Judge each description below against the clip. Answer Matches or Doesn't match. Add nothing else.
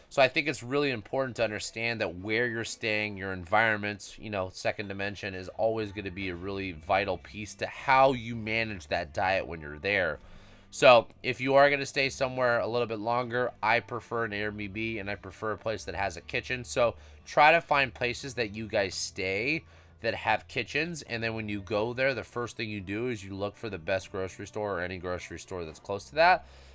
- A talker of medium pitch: Doesn't match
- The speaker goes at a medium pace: Doesn't match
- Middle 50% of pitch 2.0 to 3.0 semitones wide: Doesn't match